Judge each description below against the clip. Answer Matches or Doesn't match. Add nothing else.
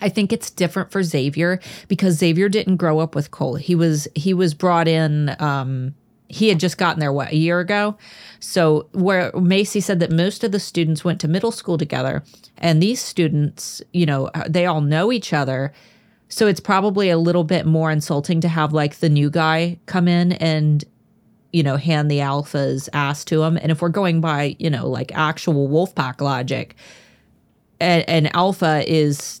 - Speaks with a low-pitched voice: Doesn't match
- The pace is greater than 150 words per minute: Matches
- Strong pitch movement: Doesn't match